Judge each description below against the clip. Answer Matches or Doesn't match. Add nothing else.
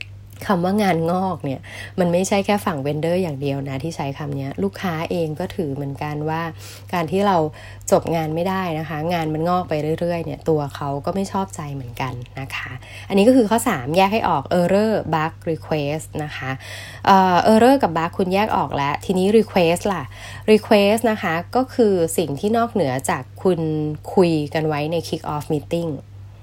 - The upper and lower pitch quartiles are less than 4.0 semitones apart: Doesn't match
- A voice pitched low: Doesn't match